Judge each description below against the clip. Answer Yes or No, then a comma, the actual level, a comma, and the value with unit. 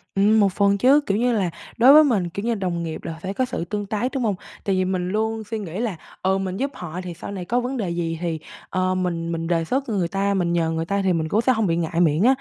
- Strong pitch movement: No, average, 4.4 semitones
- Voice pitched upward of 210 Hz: No, high, 195 Hz